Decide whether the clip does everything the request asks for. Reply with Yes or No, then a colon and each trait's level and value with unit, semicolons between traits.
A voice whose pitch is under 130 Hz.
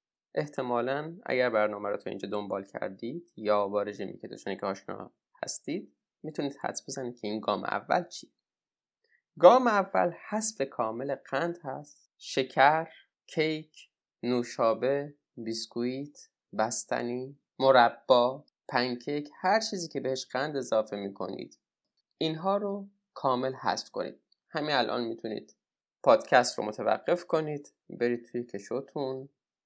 No: low, 135 Hz